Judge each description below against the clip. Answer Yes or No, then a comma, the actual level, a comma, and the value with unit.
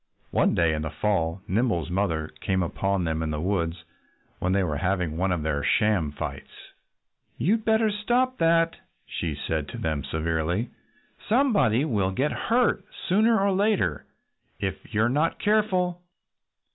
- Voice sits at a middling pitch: No, low, 100 Hz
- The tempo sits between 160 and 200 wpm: No, average, 150 wpm